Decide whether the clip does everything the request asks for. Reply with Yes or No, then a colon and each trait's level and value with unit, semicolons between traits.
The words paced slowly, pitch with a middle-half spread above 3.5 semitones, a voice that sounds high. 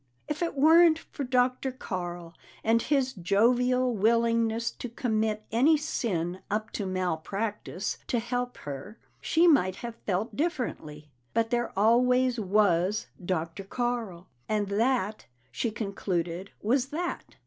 Yes: slow, 125 wpm; average, 4.7 semitones; high, 225 Hz